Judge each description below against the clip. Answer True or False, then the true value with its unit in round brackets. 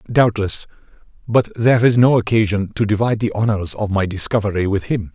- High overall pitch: False (105 Hz)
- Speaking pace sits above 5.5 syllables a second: True (5.8 syllables/s)